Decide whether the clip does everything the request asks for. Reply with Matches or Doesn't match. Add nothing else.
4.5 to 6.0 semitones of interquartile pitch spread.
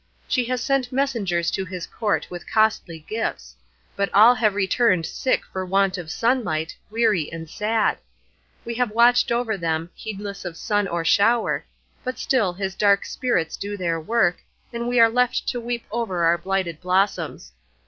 Matches